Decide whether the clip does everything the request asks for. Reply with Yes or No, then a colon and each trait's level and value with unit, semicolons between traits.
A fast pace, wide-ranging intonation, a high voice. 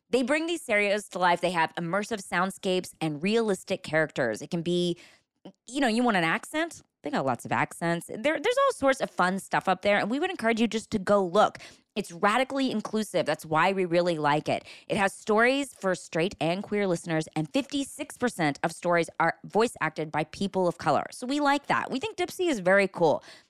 Yes: fast, 210 wpm; wide, 6.2 semitones; high, 195 Hz